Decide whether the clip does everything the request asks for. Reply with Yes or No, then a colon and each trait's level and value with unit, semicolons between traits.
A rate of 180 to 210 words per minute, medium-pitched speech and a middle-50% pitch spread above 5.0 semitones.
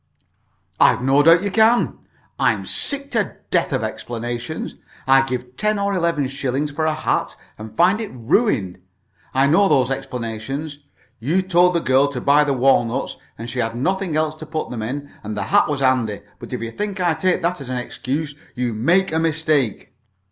Yes: average, 190 wpm; medium, 145 Hz; wide, 5.5 semitones